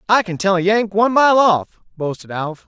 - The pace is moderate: No, fast, 225 wpm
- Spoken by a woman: No, male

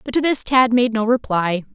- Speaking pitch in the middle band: No, high, 235 Hz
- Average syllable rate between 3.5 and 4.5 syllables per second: No, 5.1 syllables/s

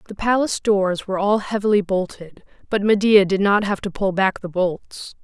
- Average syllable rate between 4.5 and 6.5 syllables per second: Yes, 5.1 syllables/s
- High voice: Yes, high, 200 Hz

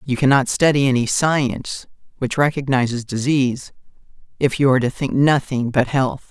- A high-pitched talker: No, low, 135 Hz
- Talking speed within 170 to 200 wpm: No, average, 150 wpm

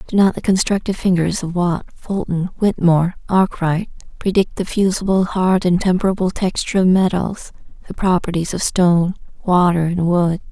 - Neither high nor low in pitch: Yes, medium, 180 Hz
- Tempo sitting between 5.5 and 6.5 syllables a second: No, 5.2 syllables/s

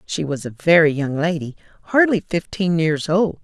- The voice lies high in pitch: No, medium, 165 Hz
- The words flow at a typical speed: Yes, average, 175 wpm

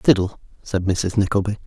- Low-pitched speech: Yes, low, 100 Hz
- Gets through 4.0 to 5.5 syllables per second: Yes, 5.2 syllables/s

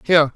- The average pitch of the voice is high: No, medium, 155 Hz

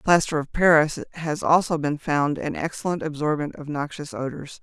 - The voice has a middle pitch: Yes, medium, 155 Hz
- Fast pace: No, average, 170 wpm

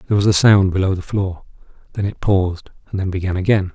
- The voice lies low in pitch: Yes, very low, 95 Hz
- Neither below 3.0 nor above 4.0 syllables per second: No, 6.7 syllables/s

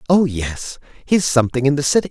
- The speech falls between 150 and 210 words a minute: Yes, average, 200 wpm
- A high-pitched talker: No, medium, 140 Hz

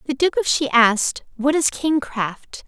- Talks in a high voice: Yes, very high, 270 Hz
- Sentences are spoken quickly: No, average, 180 wpm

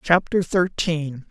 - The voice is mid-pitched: Yes, medium, 160 Hz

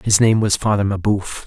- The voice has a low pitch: Yes, low, 105 Hz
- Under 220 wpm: Yes, fast, 205 wpm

